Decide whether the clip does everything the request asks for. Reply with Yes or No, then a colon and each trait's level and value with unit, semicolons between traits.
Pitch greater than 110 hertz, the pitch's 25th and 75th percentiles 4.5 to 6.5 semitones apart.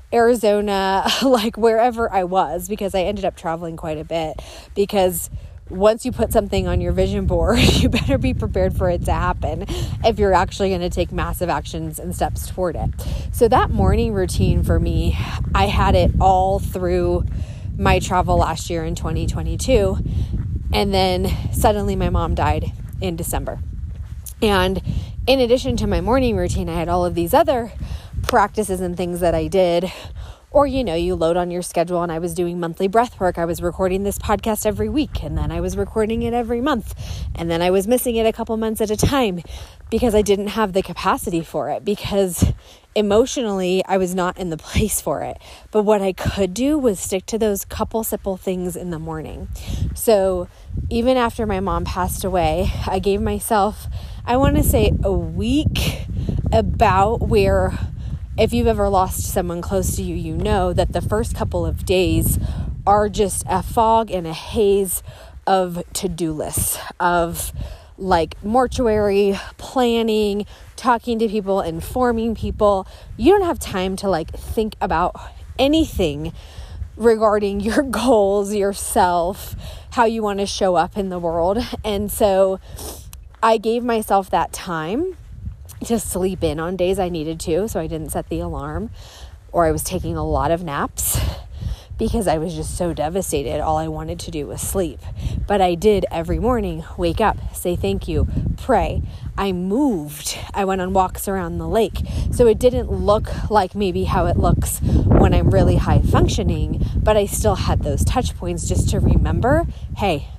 Yes: high, 190 Hz; average, 5.1 semitones